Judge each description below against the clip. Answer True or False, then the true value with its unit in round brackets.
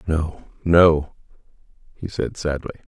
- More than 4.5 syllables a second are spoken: False (3.7 syllables/s)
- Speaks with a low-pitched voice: True (80 Hz)